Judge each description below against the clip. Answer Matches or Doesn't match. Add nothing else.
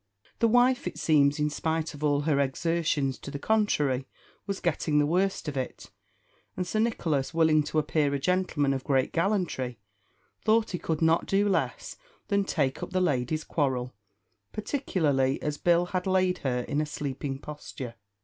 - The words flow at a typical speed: Matches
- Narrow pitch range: Doesn't match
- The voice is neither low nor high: Matches